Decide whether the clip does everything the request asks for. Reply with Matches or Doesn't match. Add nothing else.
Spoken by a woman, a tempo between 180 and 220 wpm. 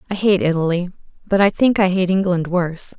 Matches